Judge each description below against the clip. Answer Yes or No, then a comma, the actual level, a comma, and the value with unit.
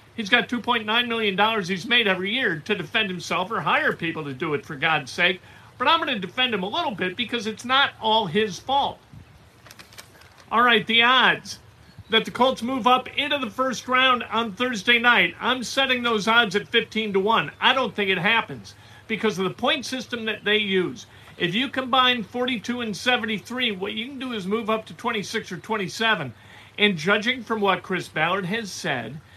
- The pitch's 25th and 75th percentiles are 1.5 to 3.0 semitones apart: No, average, 4.1 semitones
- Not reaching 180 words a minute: No, average, 200 wpm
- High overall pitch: Yes, high, 220 Hz